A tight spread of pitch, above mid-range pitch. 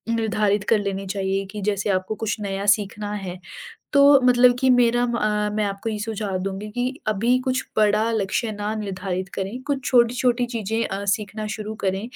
No: average, 3.0 semitones; high, 210 Hz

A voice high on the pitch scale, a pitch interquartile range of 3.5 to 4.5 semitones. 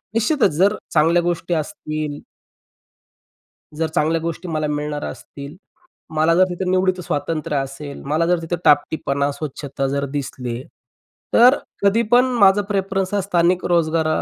No: medium, 165 Hz; average, 3.9 semitones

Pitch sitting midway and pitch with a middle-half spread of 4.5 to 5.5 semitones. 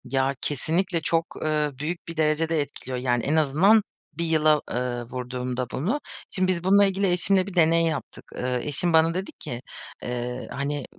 Yes: medium, 155 Hz; average, 5.0 semitones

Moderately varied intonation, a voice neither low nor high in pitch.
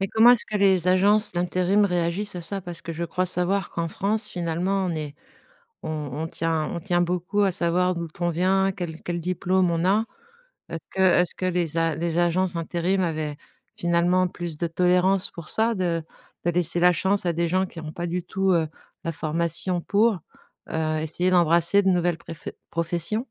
No: narrow, 2.1 semitones; medium, 175 Hz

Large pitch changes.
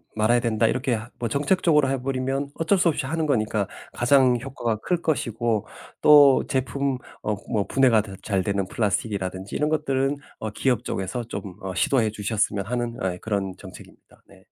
No: average, 4.4 semitones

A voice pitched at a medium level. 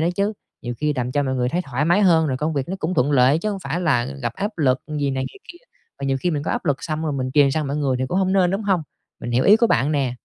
Yes: medium, 150 Hz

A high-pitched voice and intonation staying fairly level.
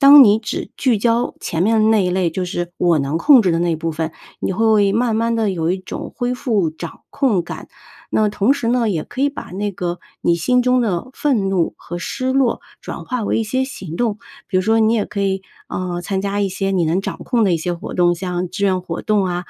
No: high, 200 Hz; average, 4.6 semitones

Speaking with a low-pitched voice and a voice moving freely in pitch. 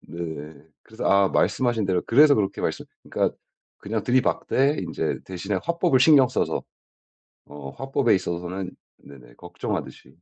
Yes: low, 100 Hz; wide, 7.0 semitones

